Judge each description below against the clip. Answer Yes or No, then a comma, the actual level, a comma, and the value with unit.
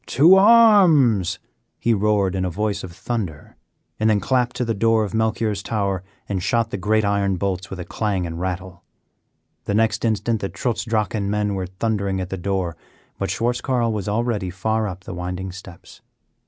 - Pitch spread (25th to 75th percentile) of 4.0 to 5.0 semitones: No, average, 3.2 semitones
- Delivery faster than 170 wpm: Yes, average, 185 wpm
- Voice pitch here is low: Yes, low, 105 Hz